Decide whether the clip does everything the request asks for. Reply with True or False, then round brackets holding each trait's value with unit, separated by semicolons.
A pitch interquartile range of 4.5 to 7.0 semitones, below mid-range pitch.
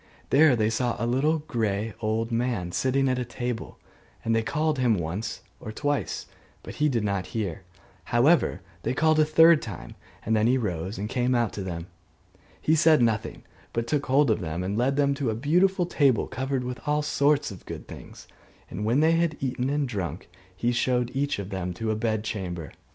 True (4.9 semitones; 120 Hz)